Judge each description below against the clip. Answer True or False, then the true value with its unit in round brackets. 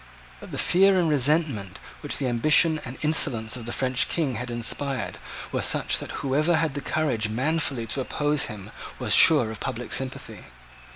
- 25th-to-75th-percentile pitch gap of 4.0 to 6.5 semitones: True (4.5 semitones)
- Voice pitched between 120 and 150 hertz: True (135 Hz)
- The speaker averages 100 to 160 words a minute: False (175 wpm)